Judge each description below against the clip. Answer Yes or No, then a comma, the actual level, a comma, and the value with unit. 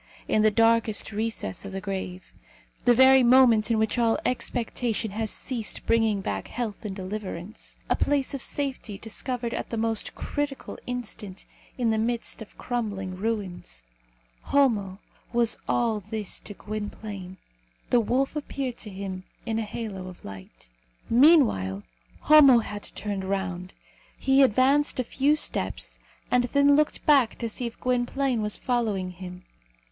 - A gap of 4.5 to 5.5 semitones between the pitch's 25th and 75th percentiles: No, average, 4.0 semitones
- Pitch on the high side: Yes, high, 225 Hz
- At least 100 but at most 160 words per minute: Yes, average, 150 wpm